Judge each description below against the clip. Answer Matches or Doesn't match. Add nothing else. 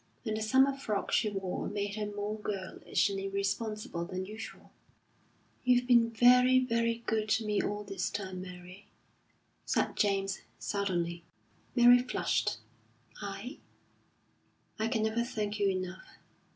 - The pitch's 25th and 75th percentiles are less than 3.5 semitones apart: Matches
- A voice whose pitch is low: Doesn't match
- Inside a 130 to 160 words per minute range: Matches